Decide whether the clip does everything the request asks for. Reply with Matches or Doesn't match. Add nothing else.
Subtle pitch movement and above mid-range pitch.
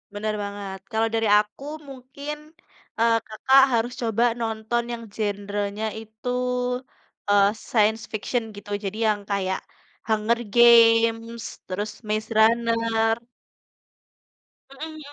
Matches